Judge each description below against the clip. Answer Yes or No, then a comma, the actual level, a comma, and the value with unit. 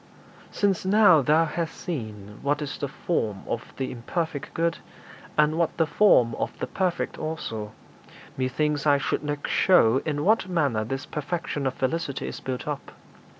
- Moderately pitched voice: Yes, medium, 150 Hz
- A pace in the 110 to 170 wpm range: Yes, average, 165 wpm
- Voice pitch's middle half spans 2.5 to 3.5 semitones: No, average, 4.2 semitones